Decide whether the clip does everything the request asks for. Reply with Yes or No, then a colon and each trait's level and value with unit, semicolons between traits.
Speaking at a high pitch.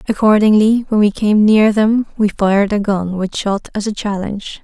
Yes: high, 210 Hz